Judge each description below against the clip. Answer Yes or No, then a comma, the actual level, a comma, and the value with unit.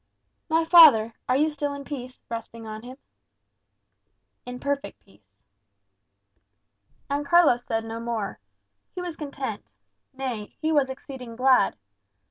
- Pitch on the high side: Yes, very high, 260 Hz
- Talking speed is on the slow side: Yes, slow, 125 wpm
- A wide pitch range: No, average, 4.0 semitones